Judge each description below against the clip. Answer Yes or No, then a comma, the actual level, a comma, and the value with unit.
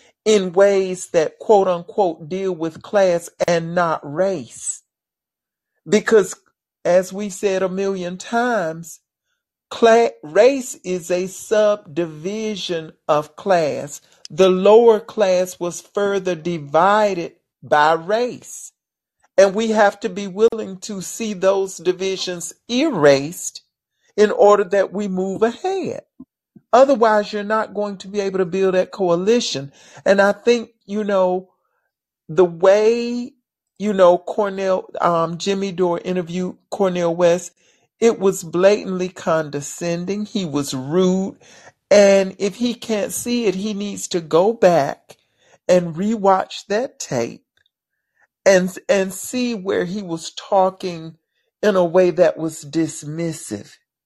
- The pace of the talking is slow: Yes, slow, 125 wpm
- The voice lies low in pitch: No, high, 190 Hz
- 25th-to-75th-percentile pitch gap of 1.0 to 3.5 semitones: Yes, average, 3.2 semitones